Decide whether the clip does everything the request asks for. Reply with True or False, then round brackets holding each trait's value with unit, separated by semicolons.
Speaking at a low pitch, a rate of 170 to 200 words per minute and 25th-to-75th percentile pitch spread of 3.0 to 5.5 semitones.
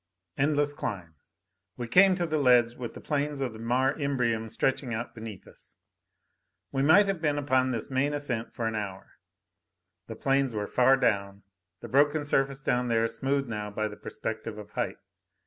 True (125 Hz; 180 wpm; 4.1 semitones)